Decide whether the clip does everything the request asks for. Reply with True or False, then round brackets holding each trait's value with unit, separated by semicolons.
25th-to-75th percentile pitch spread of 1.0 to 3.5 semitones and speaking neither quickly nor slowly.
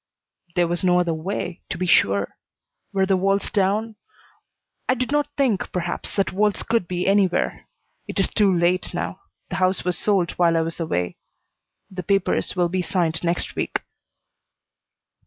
True (2.4 semitones; 165 wpm)